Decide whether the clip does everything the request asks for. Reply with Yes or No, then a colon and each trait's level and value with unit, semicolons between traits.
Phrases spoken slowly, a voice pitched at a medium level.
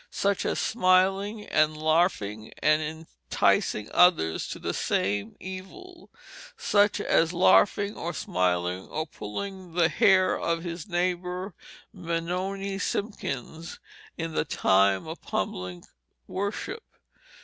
Yes: slow, 110 wpm; medium, 175 Hz